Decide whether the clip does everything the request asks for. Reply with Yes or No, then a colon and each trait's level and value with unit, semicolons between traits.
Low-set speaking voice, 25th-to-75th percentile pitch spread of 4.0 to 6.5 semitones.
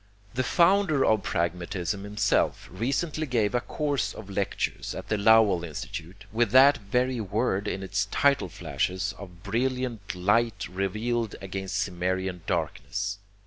Yes: low, 105 Hz; average, 4.4 semitones